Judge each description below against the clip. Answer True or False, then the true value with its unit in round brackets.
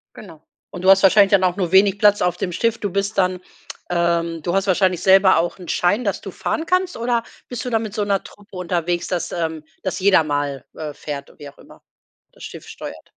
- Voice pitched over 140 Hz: True (185 Hz)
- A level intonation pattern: False (3.0 semitones)